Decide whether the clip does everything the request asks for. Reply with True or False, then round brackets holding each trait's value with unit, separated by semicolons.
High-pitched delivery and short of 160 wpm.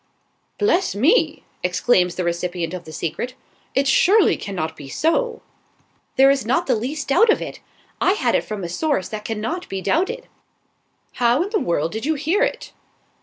False (255 Hz; 175 wpm)